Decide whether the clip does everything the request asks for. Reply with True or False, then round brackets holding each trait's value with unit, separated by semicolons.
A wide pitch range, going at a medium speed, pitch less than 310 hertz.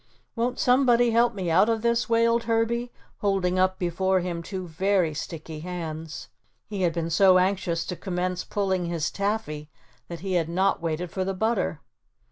False (4.4 semitones; 170 wpm; 185 Hz)